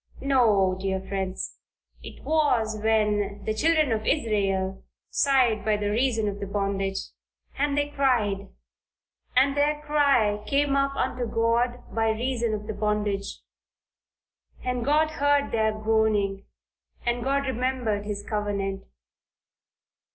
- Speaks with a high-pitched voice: Yes, high, 220 Hz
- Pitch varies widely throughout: No, average, 4.5 semitones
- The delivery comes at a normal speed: No, slow, 120 wpm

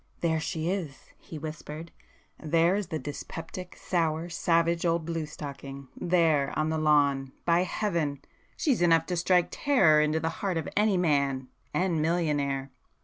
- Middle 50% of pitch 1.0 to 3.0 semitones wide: Yes, narrow, 2.6 semitones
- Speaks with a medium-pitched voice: Yes, medium, 160 Hz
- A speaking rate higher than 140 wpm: No, slow, 135 wpm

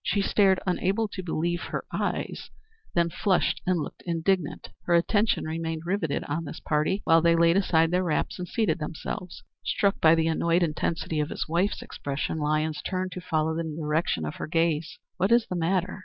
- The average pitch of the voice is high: No, medium, 170 Hz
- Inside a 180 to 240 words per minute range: Yes, average, 185 wpm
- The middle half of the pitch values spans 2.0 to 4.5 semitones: Yes, narrow, 2.5 semitones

